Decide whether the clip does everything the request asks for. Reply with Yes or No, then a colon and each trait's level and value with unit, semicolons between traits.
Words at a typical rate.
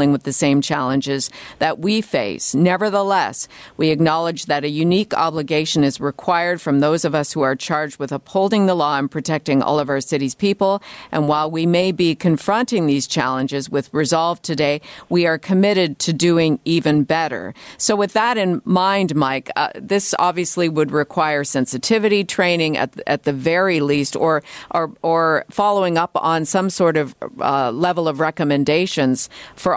Yes: average, 170 wpm